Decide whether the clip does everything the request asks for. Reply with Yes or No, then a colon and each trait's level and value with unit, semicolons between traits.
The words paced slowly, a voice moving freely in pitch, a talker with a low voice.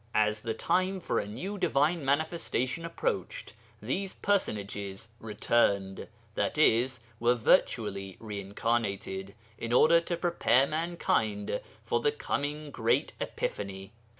Yes: slow, 115 wpm; wide, 8.2 semitones; low, 120 Hz